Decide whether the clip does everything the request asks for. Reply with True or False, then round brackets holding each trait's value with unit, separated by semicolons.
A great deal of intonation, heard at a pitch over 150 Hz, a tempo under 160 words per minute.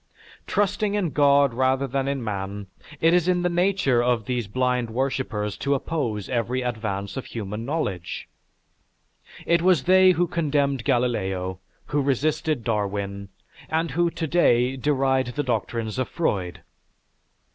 False (5.9 semitones; 130 Hz; 140 wpm)